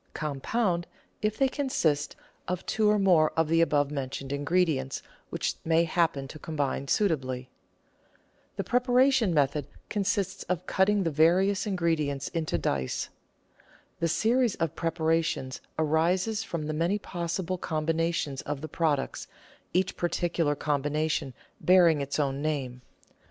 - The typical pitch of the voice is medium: Yes, medium, 165 Hz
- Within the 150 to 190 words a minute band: No, slow, 135 wpm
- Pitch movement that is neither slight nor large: Yes, average, 4.1 semitones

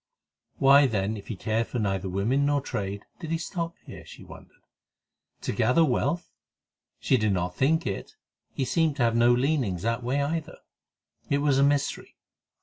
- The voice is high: No, low, 130 Hz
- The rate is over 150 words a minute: Yes, average, 175 wpm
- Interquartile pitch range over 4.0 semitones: Yes, average, 5.1 semitones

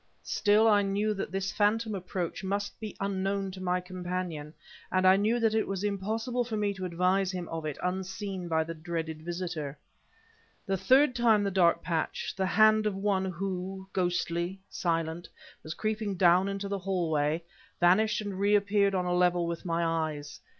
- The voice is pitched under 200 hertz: Yes, high, 190 Hz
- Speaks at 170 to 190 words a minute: Yes, average, 175 wpm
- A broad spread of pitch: No, average, 2.7 semitones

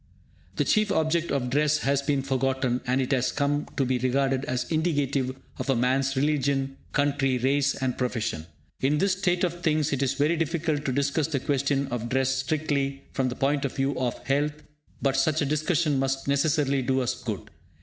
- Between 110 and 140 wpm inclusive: No, average, 190 wpm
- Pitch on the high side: No, medium, 140 Hz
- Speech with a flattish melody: Yes, narrow, 2.1 semitones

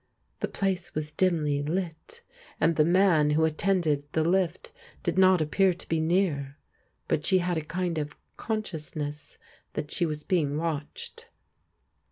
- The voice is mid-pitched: Yes, medium, 160 Hz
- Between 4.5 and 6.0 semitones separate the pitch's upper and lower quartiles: No, average, 3.4 semitones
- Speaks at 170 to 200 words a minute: No, average, 150 wpm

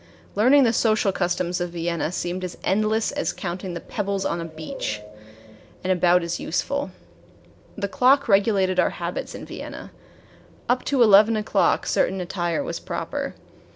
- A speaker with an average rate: Yes, average, 155 wpm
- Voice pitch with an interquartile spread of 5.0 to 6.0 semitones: No, average, 4.0 semitones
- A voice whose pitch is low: No, high, 190 Hz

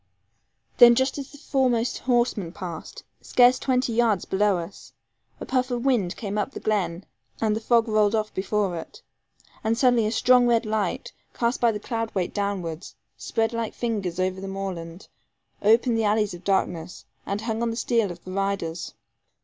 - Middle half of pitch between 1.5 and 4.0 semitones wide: Yes, average, 3.7 semitones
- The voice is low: No, high, 215 Hz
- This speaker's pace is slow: No, average, 180 wpm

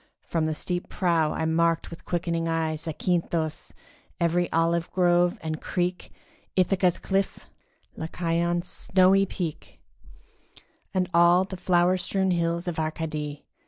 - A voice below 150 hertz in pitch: No, medium, 170 Hz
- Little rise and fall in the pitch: Yes, narrow, 1.7 semitones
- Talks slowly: Yes, slow, 125 wpm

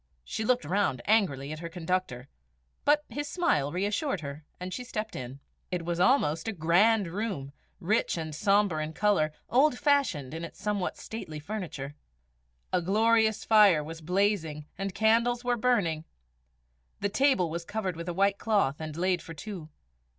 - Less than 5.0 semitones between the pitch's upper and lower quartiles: No, wide, 5.5 semitones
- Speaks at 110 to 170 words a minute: Yes, average, 165 wpm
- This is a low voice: No, medium, 185 Hz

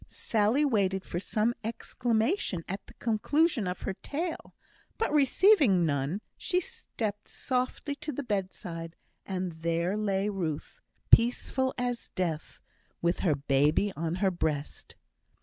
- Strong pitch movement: Yes, wide, 6.5 semitones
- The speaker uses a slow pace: Yes, slow, 130 wpm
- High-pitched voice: Yes, high, 205 Hz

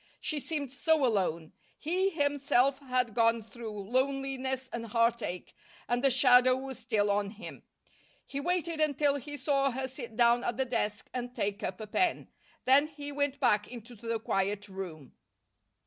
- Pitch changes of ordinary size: Yes, average, 4.0 semitones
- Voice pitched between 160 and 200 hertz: No, very high, 250 Hz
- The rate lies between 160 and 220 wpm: Yes, average, 165 wpm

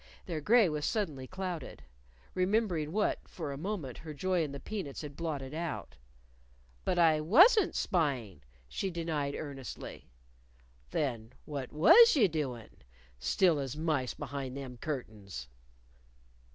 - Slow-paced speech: Yes, slow, 130 wpm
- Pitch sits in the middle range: Yes, medium, 155 Hz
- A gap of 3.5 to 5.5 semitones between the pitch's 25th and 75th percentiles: Yes, average, 5.2 semitones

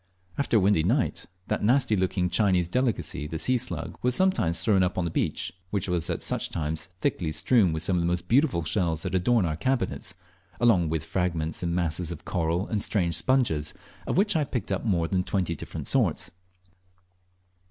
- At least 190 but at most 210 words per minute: Yes, average, 195 wpm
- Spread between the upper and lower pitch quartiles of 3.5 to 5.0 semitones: No, wide, 5.4 semitones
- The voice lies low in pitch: Yes, very low, 90 Hz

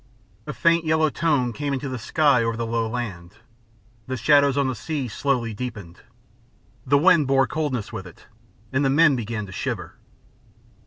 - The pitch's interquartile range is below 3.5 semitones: No, average, 4.1 semitones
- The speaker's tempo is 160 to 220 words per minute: Yes, average, 170 wpm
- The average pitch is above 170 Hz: No, low, 130 Hz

